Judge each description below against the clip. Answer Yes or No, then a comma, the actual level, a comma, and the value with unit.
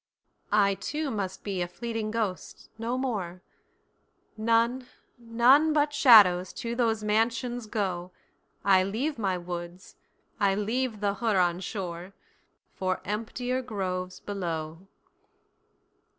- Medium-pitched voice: No, high, 210 Hz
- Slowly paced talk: Yes, slow, 95 wpm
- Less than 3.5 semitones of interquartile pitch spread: No, average, 4.2 semitones